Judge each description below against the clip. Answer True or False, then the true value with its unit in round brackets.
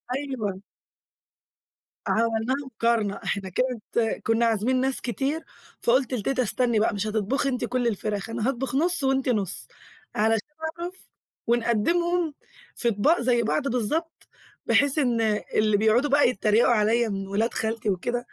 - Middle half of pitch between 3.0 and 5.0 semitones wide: True (3.6 semitones)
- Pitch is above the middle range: True (235 Hz)